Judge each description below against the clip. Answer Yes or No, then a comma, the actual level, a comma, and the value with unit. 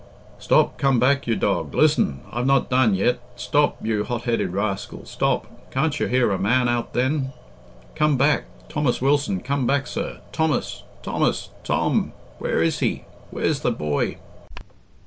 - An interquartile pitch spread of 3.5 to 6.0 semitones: Yes, average, 4.0 semitones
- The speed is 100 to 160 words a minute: Yes, average, 150 wpm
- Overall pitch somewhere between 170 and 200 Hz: No, low, 125 Hz